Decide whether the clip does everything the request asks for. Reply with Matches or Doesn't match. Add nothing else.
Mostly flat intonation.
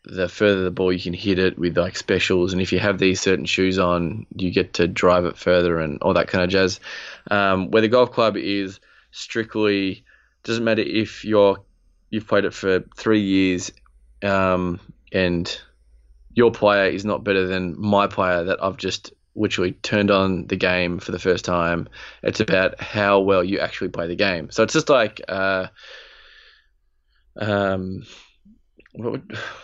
Matches